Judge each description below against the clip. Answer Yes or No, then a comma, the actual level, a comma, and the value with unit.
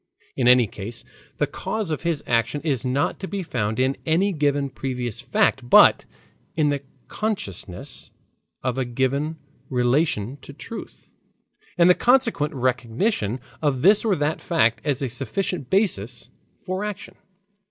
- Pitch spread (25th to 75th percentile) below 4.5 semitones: No, wide, 5.6 semitones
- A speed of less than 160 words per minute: Yes, average, 145 wpm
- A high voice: No, medium, 140 Hz